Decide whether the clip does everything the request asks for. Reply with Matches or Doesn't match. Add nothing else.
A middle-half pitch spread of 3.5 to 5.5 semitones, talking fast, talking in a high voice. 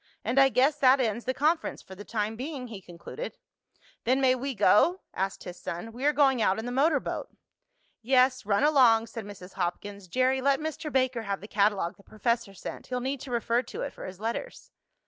Matches